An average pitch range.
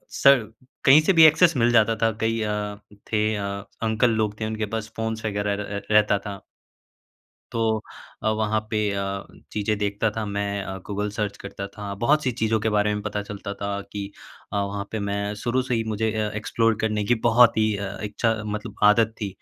No: narrow, 1.7 semitones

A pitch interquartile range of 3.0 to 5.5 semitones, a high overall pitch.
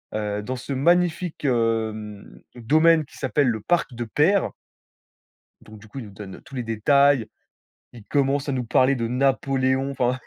No: average, 3.9 semitones; low, 130 Hz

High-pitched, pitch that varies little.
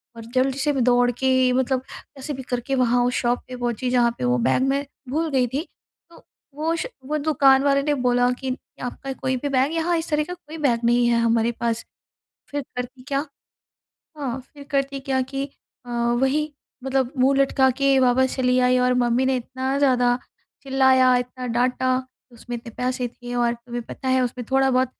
Yes: very high, 260 Hz; narrow, 2.0 semitones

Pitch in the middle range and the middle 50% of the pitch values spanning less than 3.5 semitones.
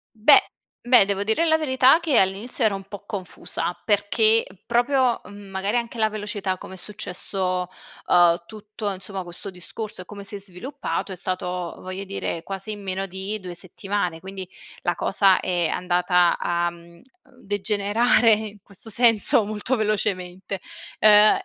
No: high, 200 Hz; average, 2.9 semitones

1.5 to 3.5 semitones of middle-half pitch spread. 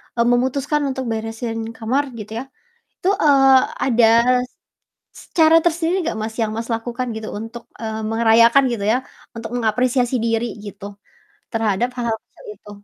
Yes: average, 2.8 semitones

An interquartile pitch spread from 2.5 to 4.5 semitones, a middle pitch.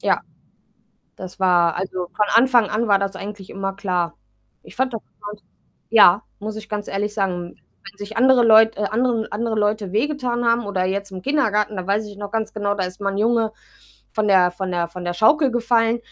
No: average, 2.8 semitones; high, 210 Hz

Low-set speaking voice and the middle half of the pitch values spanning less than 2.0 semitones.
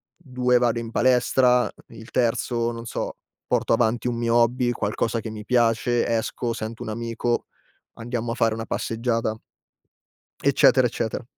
Yes: low, 115 Hz; narrow, 1.3 semitones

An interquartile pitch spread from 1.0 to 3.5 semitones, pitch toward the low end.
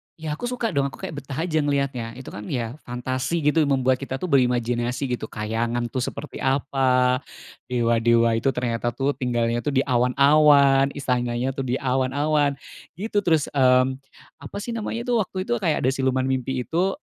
Yes: average, 2.9 semitones; low, 130 Hz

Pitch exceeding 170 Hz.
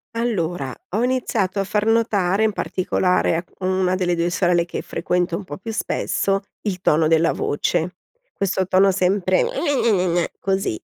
Yes: medium, 185 Hz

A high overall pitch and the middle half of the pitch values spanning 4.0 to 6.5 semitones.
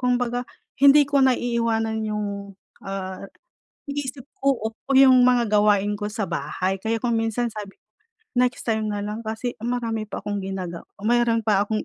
No: high, 225 Hz; average, 3.1 semitones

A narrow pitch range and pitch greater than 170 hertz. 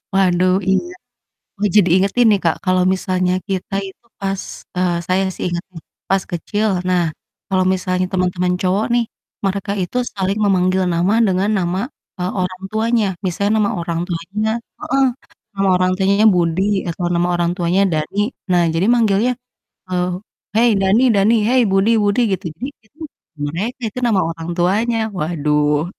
Yes: narrow, 2.3 semitones; medium, 185 Hz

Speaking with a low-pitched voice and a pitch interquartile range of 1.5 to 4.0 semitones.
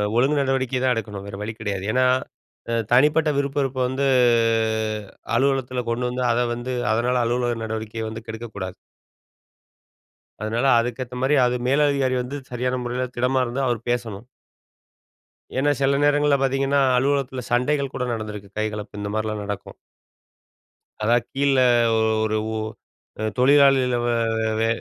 Yes: low, 125 Hz; average, 3.3 semitones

